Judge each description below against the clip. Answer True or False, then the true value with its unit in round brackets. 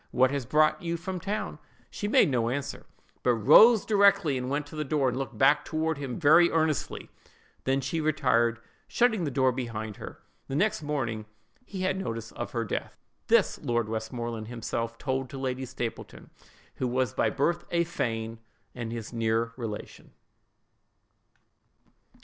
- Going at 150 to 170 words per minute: True (160 wpm)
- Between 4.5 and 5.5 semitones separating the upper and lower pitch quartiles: True (5.2 semitones)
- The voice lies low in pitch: True (130 Hz)